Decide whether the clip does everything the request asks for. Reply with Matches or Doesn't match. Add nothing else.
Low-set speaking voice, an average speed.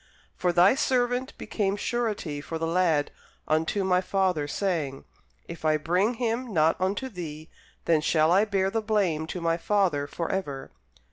Doesn't match